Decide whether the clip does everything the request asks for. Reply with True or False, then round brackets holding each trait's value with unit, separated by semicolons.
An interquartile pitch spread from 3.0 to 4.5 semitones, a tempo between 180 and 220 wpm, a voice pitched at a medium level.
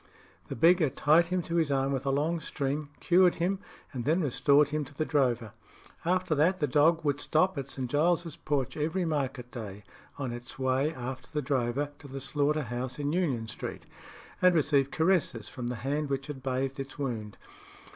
True (3.4 semitones; 190 wpm; 145 Hz)